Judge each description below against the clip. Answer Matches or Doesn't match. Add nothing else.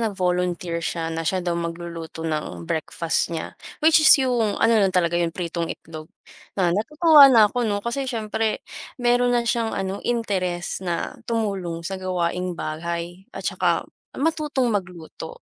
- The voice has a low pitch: Doesn't match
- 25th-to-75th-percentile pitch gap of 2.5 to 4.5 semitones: Doesn't match